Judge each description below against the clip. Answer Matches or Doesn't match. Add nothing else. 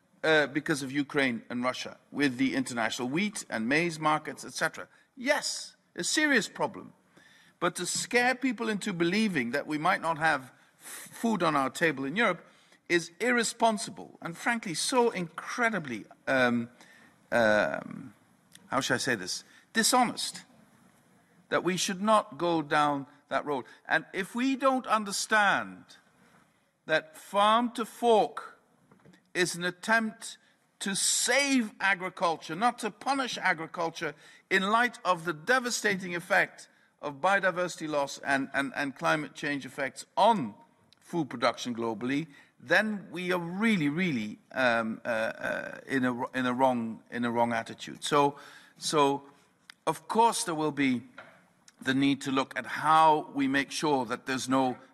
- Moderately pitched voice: Matches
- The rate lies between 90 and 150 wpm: Matches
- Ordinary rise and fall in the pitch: Doesn't match